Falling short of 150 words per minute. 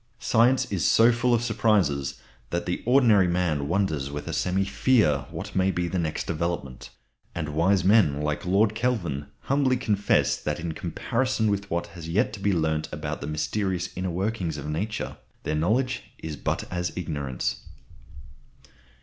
No: average, 165 wpm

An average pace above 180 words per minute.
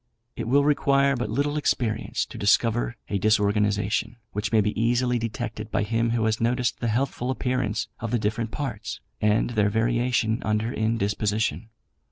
No: average, 160 wpm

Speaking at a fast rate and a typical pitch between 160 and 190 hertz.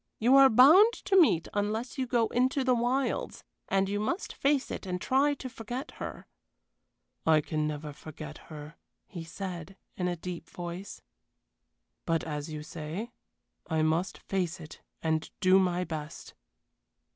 No: average, 155 wpm; medium, 185 Hz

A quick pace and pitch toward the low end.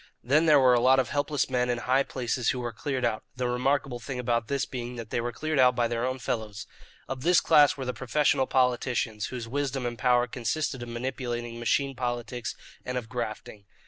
Yes: fast, 210 wpm; low, 125 Hz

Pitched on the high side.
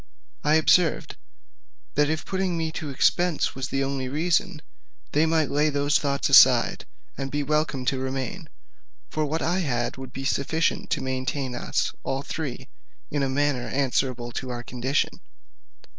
No: medium, 140 Hz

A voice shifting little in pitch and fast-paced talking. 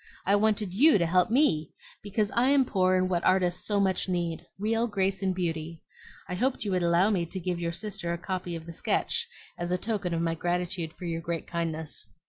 No: average, 3.1 semitones; fast, 220 wpm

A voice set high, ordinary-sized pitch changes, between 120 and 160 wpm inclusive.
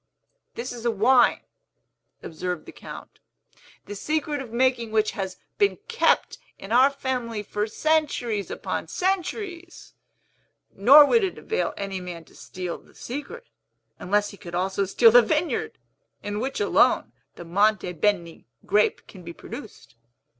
No: high, 225 Hz; wide, 6.5 semitones; average, 145 wpm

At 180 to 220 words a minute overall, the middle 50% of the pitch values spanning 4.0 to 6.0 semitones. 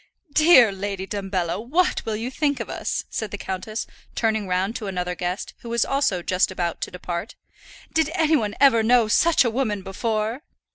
Yes: average, 185 wpm; average, 4.7 semitones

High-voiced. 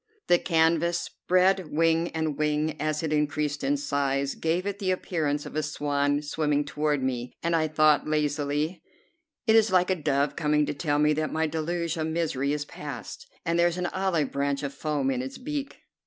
No: medium, 155 Hz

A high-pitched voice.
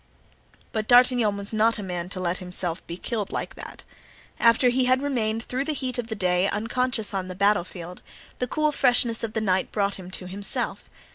Yes: high, 215 Hz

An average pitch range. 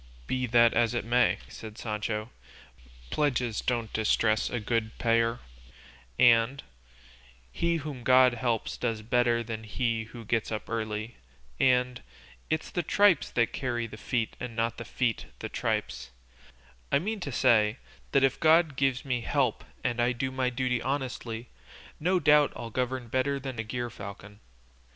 No: narrow, 2.3 semitones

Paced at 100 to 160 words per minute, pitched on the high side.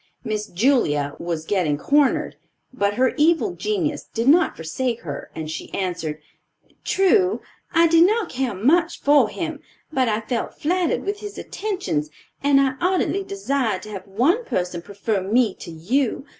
Yes: average, 155 wpm; very high, 255 Hz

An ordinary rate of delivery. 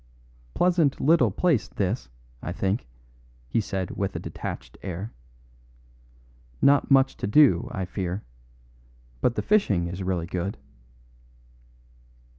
No: slow, 115 wpm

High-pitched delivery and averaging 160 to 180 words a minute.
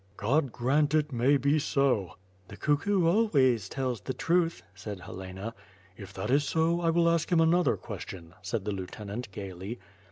No: low, 130 Hz; average, 170 wpm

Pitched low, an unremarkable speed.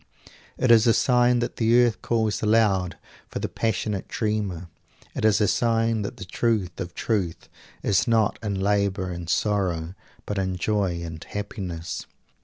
Yes: low, 105 Hz; average, 160 wpm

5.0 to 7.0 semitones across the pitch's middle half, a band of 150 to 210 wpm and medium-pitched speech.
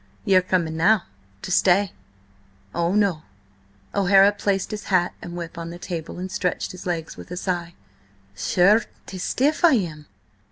No: average, 2.7 semitones; average, 160 wpm; medium, 180 Hz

